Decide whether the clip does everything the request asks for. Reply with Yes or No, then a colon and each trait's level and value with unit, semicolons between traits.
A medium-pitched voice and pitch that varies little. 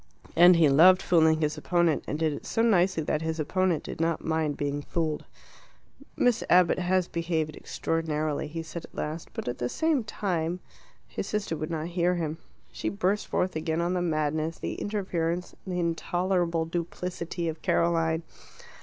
Yes: medium, 165 Hz; narrow, 2.2 semitones